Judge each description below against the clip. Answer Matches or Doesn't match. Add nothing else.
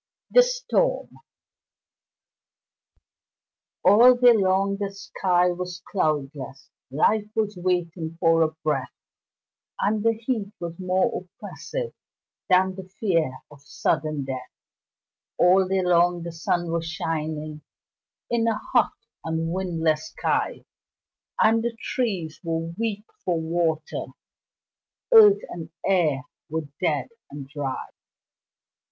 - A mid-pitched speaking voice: Matches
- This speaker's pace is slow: Matches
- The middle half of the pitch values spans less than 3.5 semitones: Doesn't match